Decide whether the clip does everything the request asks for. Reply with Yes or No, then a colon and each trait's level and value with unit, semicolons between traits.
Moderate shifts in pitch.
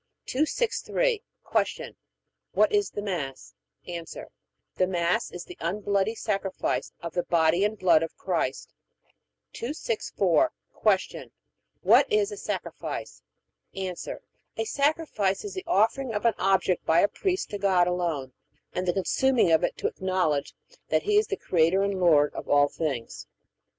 No: wide, 5.8 semitones